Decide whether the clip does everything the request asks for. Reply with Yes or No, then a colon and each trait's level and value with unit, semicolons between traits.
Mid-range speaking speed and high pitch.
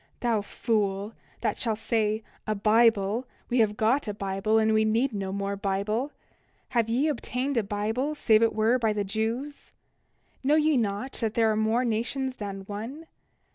Yes: average, 180 wpm; high, 220 Hz